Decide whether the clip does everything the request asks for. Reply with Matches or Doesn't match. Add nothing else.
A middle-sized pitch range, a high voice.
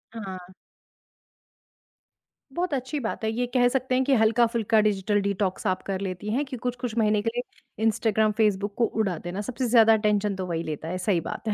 Matches